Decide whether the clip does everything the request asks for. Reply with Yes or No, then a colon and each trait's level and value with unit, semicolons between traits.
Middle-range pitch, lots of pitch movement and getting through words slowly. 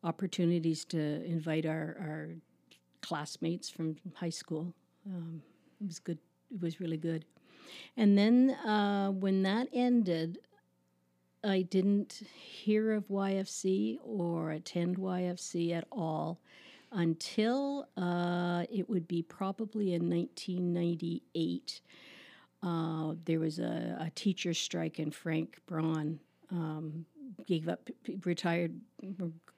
No: medium, 175 Hz; average, 3.4 semitones; slow, 115 wpm